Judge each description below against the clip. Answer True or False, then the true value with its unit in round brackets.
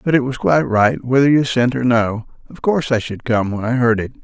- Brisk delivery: True (270 wpm)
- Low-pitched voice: True (125 Hz)